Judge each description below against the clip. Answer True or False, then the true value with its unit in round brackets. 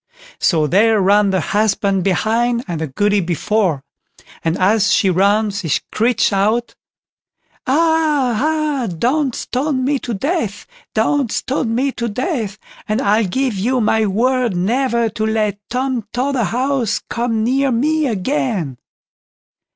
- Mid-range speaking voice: False (225 Hz)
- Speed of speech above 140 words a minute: False (135 wpm)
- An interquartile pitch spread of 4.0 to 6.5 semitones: True (4.5 semitones)